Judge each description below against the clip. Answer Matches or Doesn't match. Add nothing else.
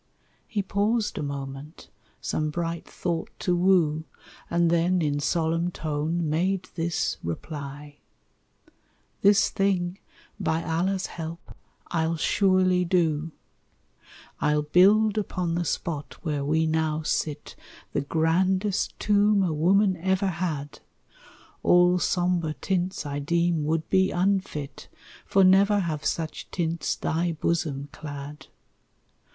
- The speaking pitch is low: Doesn't match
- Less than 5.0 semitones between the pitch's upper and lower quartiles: Matches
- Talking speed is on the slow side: Matches